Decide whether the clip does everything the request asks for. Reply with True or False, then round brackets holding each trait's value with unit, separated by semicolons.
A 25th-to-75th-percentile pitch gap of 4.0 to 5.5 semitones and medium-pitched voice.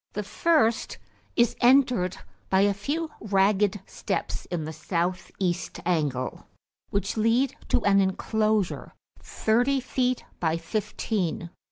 False (4.7 semitones; 205 Hz)